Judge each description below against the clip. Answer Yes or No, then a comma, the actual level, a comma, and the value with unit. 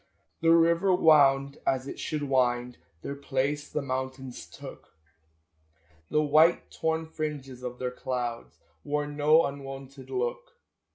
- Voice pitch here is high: No, medium, 140 Hz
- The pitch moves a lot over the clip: No, average, 3.1 semitones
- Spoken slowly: Yes, slow, 125 wpm